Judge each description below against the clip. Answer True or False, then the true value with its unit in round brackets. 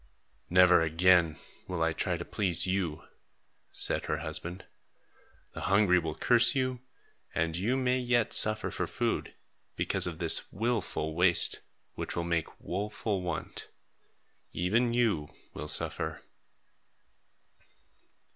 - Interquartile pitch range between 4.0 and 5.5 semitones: True (4.6 semitones)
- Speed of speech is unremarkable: False (120 wpm)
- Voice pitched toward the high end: False (90 Hz)